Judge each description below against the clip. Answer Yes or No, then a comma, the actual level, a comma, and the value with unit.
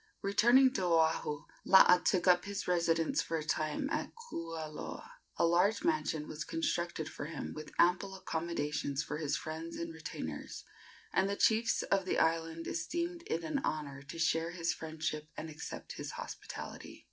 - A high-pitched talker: No, medium, 165 Hz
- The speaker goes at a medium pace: Yes, average, 160 wpm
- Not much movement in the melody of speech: No, average, 3.3 semitones